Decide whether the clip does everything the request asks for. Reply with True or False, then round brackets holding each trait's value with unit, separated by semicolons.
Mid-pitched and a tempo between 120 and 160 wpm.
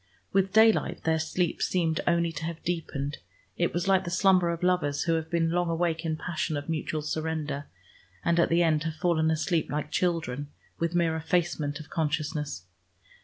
False (165 Hz; 180 wpm)